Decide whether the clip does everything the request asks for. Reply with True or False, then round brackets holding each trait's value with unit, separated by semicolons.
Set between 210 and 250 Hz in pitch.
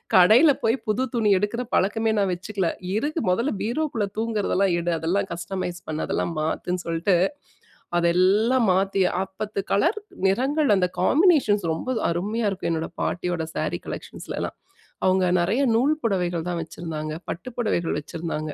False (195 Hz)